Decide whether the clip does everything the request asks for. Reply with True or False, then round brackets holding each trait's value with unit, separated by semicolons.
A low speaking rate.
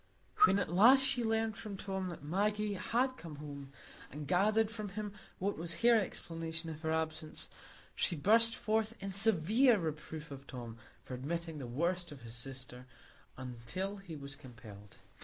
False (165 wpm)